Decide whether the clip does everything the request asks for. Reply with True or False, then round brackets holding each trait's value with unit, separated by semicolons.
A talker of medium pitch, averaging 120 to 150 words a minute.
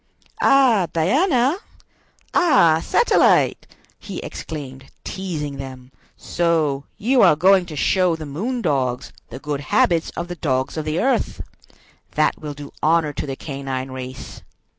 True (155 Hz; 140 wpm)